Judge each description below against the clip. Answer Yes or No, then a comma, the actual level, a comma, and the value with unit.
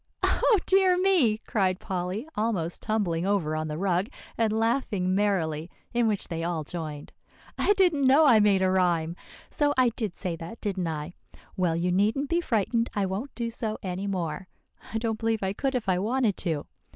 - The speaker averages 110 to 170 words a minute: No, average, 190 wpm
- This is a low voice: No, high, 200 Hz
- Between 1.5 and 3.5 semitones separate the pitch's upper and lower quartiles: No, average, 4.7 semitones